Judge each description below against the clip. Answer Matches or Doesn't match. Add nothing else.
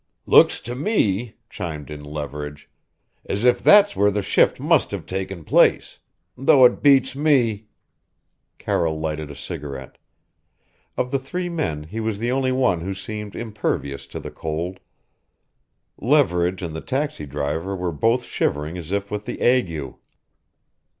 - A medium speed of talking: Matches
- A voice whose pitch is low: Matches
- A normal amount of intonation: Doesn't match